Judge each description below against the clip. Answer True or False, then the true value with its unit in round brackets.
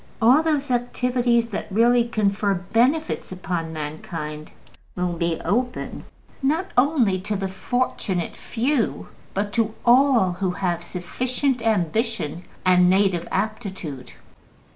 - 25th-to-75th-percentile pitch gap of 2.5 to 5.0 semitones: False (5.4 semitones)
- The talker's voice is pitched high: True (210 Hz)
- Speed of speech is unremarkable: False (115 wpm)